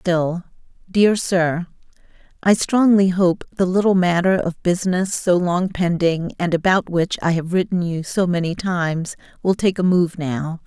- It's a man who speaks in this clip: No, female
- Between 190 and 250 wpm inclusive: No, average, 160 wpm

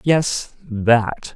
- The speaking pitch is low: Yes, low, 120 Hz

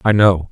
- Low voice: Yes, very low, 95 Hz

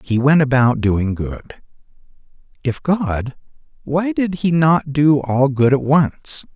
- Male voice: Yes, male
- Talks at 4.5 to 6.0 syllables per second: No, 3.5 syllables/s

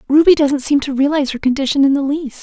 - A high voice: Yes, very high, 280 Hz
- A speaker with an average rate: No, fast, 250 wpm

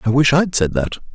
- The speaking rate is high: Yes, fast, 260 wpm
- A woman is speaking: No, male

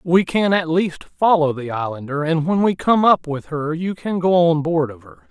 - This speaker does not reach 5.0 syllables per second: Yes, 4.6 syllables/s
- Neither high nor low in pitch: Yes, medium, 160 Hz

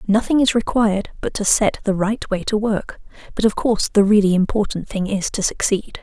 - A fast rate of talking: Yes, fast, 210 wpm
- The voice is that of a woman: Yes, female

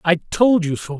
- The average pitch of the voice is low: No, medium, 180 Hz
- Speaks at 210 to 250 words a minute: Yes, fast, 240 wpm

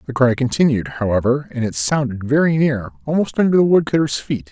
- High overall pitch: No, low, 130 Hz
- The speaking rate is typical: Yes, average, 185 wpm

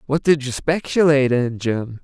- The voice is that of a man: Yes, male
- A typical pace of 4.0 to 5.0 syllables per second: Yes, 4.8 syllables/s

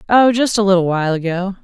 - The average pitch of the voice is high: Yes, high, 195 Hz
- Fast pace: Yes, fast, 220 wpm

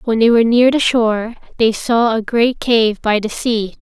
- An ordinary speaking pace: No, fast, 220 wpm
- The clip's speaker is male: No, female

